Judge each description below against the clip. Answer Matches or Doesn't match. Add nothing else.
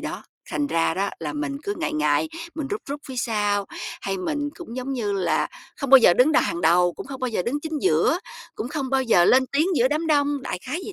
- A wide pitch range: Matches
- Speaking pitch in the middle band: Doesn't match